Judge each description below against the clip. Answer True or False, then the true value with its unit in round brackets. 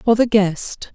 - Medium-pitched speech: False (210 Hz)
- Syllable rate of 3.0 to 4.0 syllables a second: True (3.7 syllables/s)